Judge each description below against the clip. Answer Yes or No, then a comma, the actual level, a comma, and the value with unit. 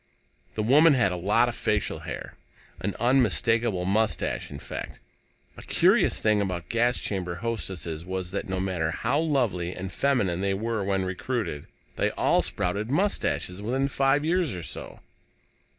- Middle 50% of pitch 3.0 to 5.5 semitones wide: Yes, average, 5.2 semitones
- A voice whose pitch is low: Yes, low, 105 Hz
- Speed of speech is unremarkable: Yes, average, 155 wpm